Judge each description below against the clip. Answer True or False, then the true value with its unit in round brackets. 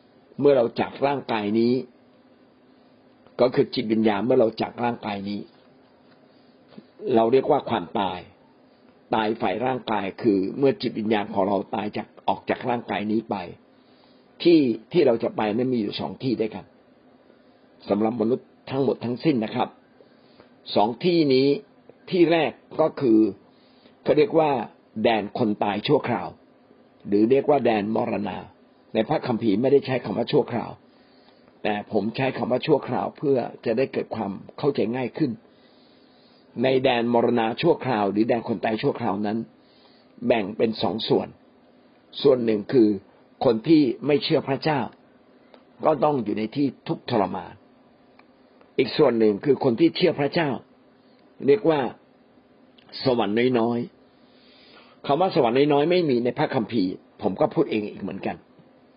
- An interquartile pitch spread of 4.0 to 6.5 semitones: True (4.3 semitones)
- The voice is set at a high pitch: False (120 Hz)